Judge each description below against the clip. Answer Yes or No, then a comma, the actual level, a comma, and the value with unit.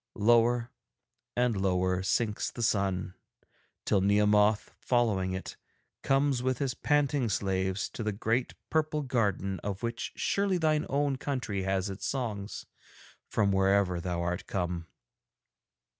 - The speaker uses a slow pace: Yes, slow, 130 wpm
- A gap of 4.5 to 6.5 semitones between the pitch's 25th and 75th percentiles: Yes, average, 4.8 semitones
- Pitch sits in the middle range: No, low, 105 Hz